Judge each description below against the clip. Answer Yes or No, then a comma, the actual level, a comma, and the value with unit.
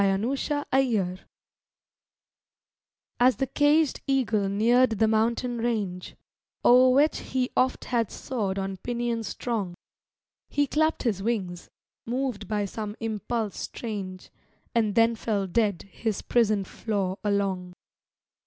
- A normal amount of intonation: Yes, average, 3.9 semitones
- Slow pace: Yes, slow, 125 wpm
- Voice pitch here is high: Yes, high, 225 Hz